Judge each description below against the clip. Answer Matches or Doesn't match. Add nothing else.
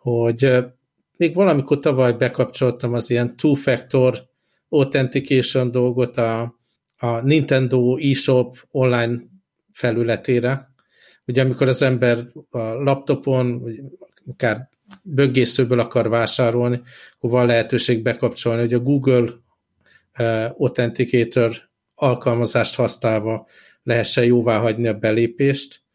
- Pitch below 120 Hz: Doesn't match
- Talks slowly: Matches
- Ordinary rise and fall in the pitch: Doesn't match